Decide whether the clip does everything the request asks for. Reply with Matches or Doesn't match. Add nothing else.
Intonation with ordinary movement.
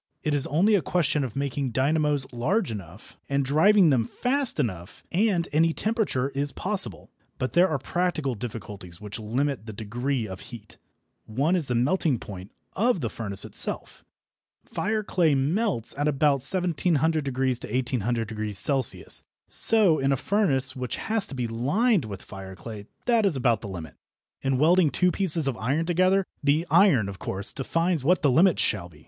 Doesn't match